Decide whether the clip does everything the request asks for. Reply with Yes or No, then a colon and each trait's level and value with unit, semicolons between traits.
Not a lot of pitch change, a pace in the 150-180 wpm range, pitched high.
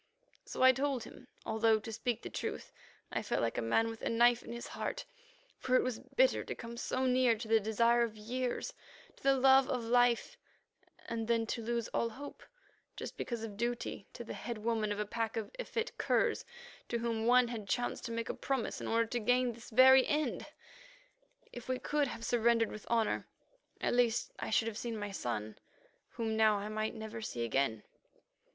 No: narrow, 2.1 semitones; average, 200 wpm; high, 230 Hz